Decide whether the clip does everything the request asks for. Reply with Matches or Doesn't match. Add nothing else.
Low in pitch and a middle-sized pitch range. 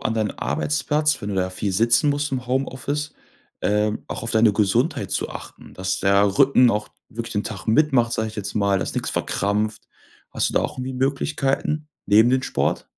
Matches